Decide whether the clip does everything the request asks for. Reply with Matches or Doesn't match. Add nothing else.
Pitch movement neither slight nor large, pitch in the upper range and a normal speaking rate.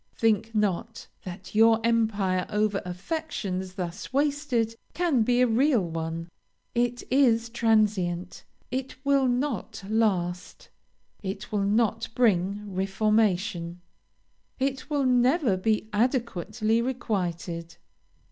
Doesn't match